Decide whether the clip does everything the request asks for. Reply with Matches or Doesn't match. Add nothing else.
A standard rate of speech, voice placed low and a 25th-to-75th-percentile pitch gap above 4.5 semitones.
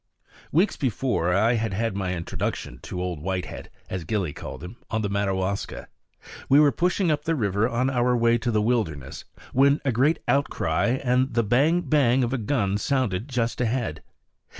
Matches